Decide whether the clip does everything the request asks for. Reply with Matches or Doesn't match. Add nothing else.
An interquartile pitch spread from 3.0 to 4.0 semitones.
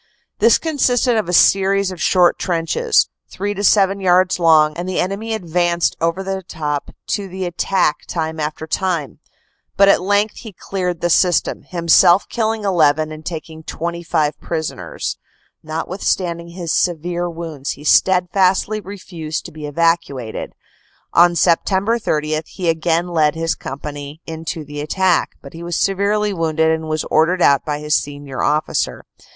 Matches